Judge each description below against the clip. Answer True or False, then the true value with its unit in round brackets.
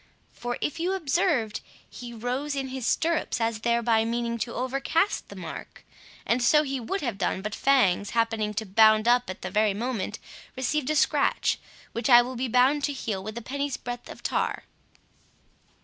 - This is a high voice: True (240 Hz)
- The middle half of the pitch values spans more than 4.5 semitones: False (3.5 semitones)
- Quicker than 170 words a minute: True (180 wpm)